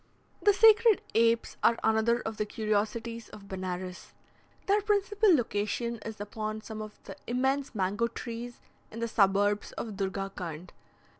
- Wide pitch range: No, average, 2.9 semitones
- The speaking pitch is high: Yes, high, 220 Hz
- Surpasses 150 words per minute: No, average, 140 wpm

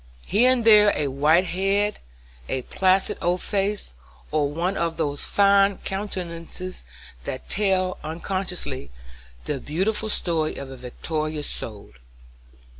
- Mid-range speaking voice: Yes, medium, 180 Hz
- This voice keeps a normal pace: No, slow, 120 wpm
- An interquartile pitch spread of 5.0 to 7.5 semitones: No, average, 4.5 semitones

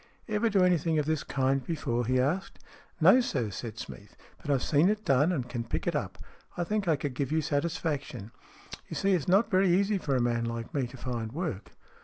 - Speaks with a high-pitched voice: No, medium, 145 Hz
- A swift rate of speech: Yes, fast, 235 wpm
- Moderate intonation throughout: No, wide, 6.4 semitones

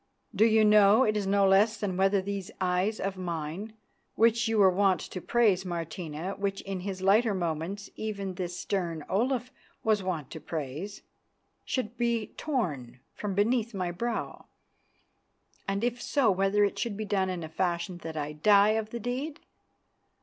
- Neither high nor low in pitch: No, high, 195 Hz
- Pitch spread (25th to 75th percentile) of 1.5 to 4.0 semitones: Yes, average, 3.3 semitones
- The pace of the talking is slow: No, average, 170 wpm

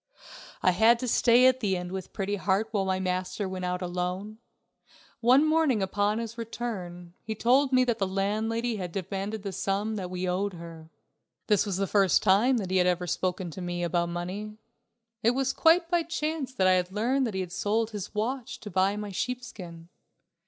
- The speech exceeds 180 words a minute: Yes, average, 200 wpm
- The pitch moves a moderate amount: Yes, average, 4.1 semitones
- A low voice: No, high, 200 Hz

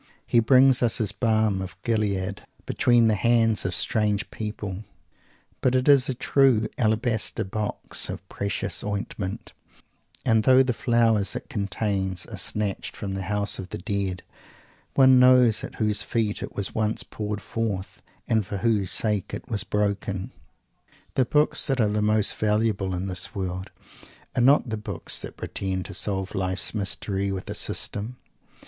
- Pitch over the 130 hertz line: No, low, 105 Hz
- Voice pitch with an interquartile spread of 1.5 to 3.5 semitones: Yes, average, 2.9 semitones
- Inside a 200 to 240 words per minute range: No, average, 160 wpm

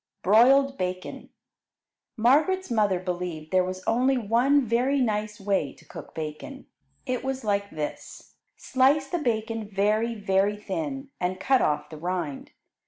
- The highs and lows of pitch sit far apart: Yes, wide, 6.2 semitones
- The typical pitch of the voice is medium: No, high, 215 Hz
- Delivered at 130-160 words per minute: Yes, average, 140 wpm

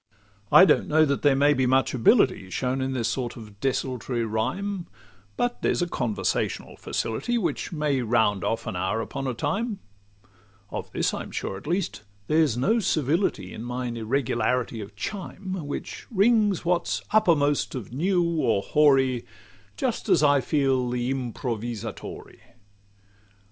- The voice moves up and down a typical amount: No, wide, 6.1 semitones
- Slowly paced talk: No, average, 150 wpm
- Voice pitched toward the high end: No, low, 135 Hz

